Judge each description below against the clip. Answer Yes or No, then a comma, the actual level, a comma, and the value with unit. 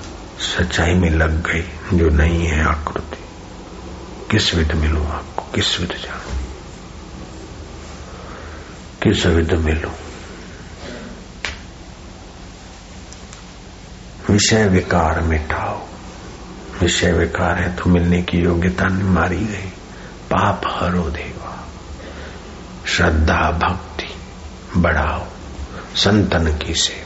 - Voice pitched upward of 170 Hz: No, very low, 85 Hz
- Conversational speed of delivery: No, slow, 85 wpm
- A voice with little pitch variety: Yes, narrow, 2.1 semitones